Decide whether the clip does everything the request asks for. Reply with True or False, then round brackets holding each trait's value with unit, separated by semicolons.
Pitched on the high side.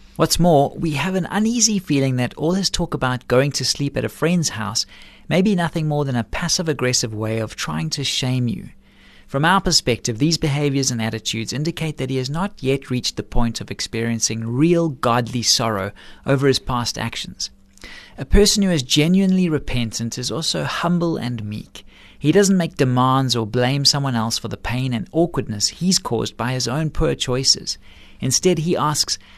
False (130 Hz)